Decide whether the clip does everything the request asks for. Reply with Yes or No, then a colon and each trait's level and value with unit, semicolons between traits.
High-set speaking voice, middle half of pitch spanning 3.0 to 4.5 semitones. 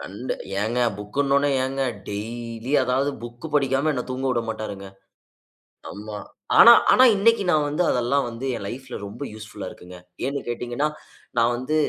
No: low, 125 Hz; average, 3.8 semitones